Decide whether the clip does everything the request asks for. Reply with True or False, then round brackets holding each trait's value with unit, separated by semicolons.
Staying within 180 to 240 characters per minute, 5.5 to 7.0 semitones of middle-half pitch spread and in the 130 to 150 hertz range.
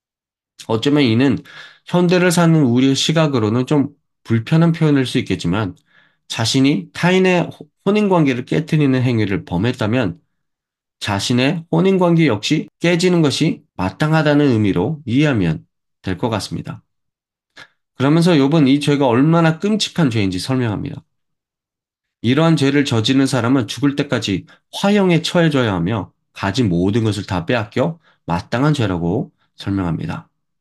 False (300 characters per minute; 6.4 semitones; 135 Hz)